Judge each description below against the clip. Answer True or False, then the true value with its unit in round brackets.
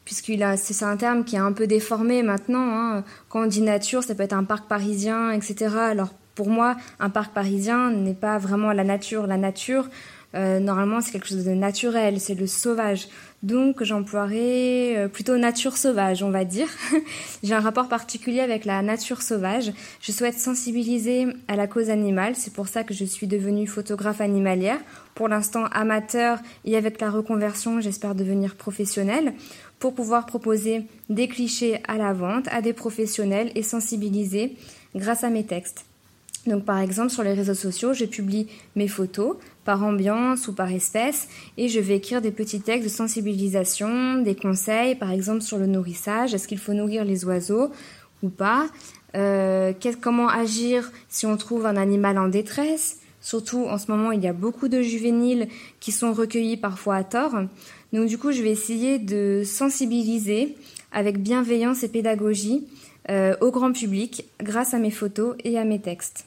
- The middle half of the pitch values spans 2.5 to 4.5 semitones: True (2.8 semitones)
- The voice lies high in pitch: True (215 Hz)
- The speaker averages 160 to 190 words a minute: True (175 wpm)